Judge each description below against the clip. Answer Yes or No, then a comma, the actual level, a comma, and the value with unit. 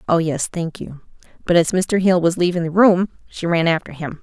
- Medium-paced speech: No, fast, 215 wpm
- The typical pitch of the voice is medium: Yes, medium, 170 Hz